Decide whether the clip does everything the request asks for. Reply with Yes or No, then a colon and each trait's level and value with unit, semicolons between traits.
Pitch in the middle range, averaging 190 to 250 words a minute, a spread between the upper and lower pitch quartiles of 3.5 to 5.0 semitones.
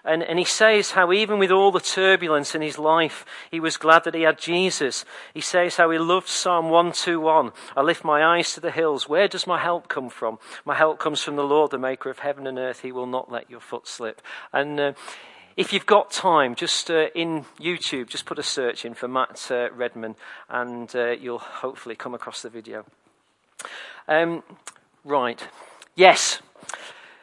Yes: medium, 160 Hz; average, 195 wpm; average, 4.1 semitones